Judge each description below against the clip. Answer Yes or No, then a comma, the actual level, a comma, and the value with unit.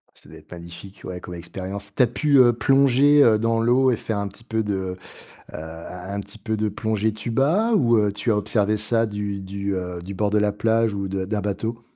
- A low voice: Yes, low, 105 Hz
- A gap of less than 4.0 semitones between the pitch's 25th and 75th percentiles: Yes, average, 2.8 semitones